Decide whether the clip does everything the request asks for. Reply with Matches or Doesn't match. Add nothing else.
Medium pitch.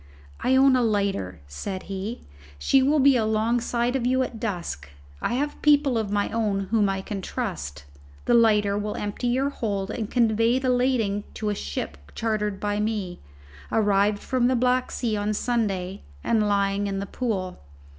Doesn't match